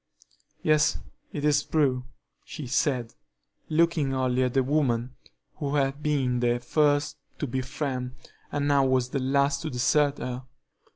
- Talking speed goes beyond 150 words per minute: No, average, 140 wpm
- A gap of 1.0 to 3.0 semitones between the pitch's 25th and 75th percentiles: Yes, narrow, 2.5 semitones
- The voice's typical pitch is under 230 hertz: Yes, low, 135 Hz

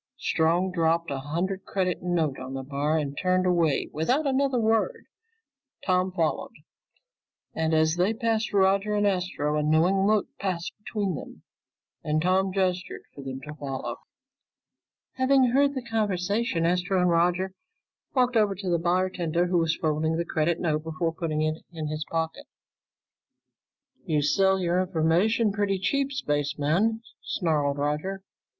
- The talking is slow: No, average, 145 wpm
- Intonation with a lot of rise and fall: No, average, 3.9 semitones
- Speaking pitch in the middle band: Yes, medium, 180 Hz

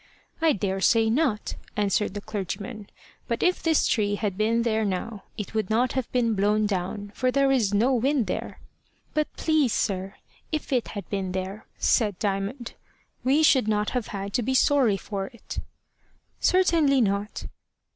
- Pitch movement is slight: No, average, 4.2 semitones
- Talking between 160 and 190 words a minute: Yes, average, 165 wpm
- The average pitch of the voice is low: No, high, 220 Hz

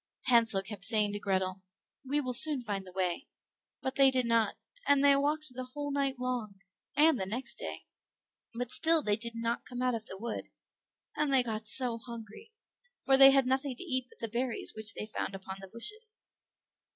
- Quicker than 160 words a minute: Yes, average, 200 wpm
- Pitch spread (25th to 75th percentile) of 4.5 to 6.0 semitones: No, average, 4.0 semitones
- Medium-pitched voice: No, high, 245 Hz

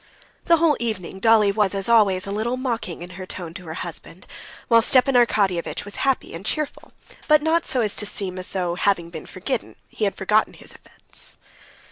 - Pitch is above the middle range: Yes, high, 205 Hz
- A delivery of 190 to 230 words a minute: Yes, average, 195 wpm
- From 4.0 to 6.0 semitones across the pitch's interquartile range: Yes, average, 4.4 semitones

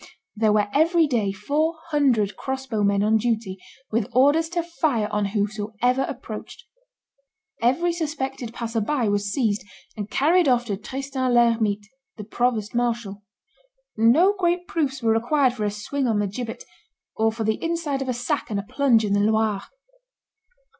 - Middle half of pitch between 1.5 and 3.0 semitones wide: No, average, 4.6 semitones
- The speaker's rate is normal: Yes, average, 160 wpm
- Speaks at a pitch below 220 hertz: No, high, 235 Hz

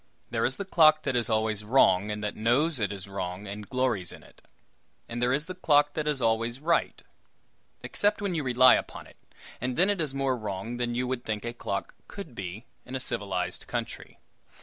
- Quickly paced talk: Yes, fast, 210 wpm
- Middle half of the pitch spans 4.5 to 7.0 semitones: Yes, wide, 5.5 semitones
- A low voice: Yes, low, 120 Hz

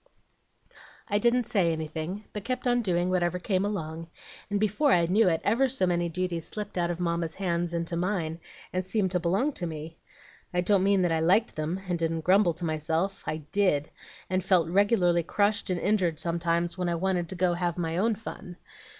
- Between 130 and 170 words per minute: No, fast, 205 wpm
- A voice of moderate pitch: Yes, medium, 180 Hz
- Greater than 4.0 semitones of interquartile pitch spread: No, average, 3.1 semitones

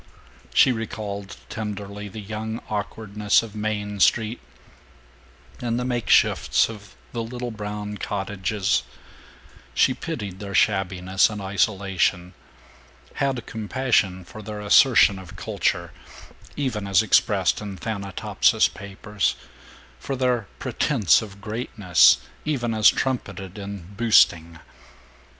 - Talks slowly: Yes, slow, 110 wpm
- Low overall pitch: Yes, low, 105 Hz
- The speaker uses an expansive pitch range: No, narrow, 2.4 semitones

